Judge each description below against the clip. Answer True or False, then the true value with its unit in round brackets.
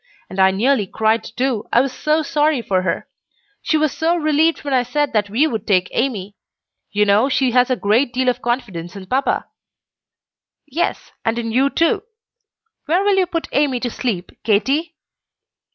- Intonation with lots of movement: True (5.8 semitones)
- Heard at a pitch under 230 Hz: False (250 Hz)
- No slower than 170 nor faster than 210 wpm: True (180 wpm)